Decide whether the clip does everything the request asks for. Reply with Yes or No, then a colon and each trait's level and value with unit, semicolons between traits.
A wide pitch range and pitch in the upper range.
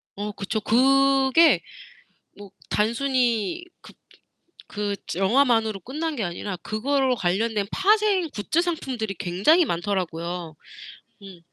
Yes: wide, 5.8 semitones; high, 225 Hz